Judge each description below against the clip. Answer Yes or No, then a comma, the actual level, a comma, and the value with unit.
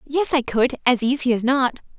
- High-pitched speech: Yes, very high, 255 Hz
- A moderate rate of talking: No, fast, 210 wpm